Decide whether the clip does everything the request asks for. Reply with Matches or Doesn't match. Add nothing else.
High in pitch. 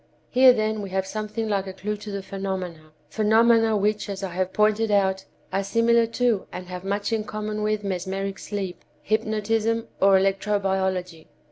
Matches